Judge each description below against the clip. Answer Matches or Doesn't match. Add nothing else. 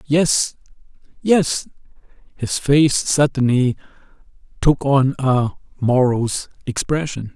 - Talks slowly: Matches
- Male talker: Matches